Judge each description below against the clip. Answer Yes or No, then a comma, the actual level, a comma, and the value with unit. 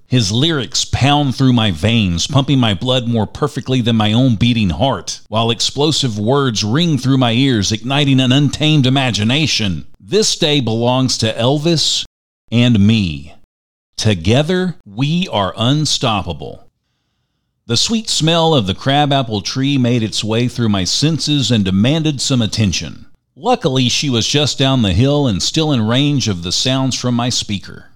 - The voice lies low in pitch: Yes, low, 125 Hz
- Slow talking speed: No, average, 155 wpm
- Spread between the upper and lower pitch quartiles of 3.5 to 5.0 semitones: Yes, average, 4.5 semitones